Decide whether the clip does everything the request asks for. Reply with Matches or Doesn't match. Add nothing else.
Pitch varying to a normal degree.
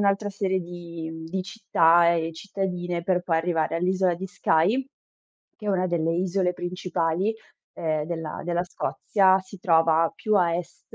Doesn't match